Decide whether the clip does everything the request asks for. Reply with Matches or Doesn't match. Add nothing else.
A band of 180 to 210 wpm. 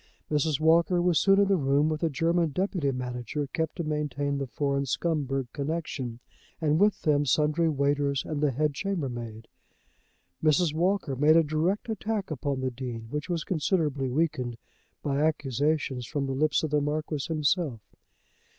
Doesn't match